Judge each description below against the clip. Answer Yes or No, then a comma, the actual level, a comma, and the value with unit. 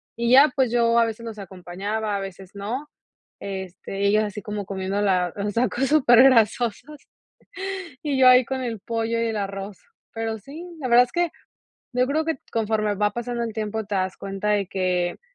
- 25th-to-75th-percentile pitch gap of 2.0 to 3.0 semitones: No, average, 3.6 semitones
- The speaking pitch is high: Yes, high, 220 Hz